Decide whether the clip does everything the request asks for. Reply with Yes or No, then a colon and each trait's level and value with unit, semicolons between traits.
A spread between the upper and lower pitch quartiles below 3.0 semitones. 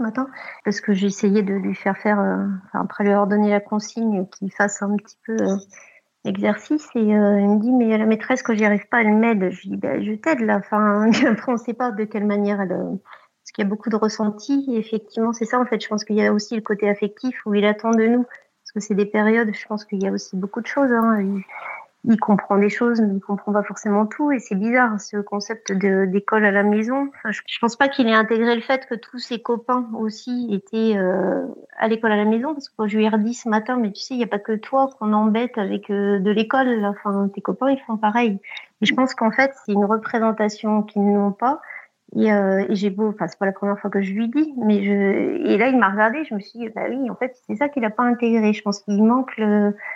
Yes: narrow, 2.5 semitones